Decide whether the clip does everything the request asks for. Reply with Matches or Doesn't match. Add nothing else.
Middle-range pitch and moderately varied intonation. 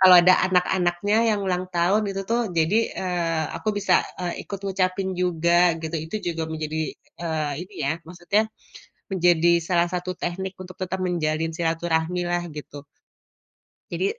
Doesn't match